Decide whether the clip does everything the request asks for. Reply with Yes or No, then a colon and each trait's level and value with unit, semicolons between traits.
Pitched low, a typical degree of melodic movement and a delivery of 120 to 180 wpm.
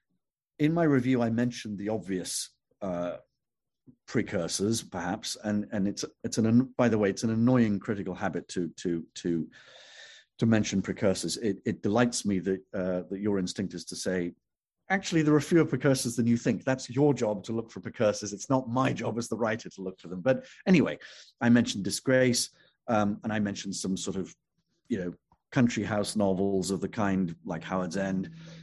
No: low, 105 Hz; average, 4.2 semitones; average, 190 wpm